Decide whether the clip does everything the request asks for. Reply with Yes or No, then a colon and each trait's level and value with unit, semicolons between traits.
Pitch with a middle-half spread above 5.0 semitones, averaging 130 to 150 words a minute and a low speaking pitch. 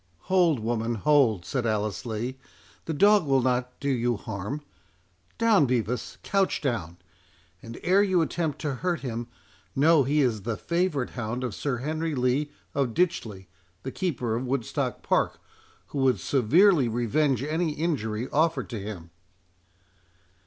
Yes: wide, 5.5 semitones; average, 140 wpm; low, 130 Hz